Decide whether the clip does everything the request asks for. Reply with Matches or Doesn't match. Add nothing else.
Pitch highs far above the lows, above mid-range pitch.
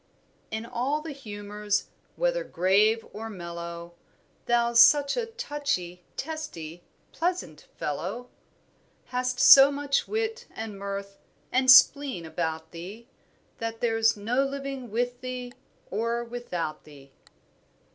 Matches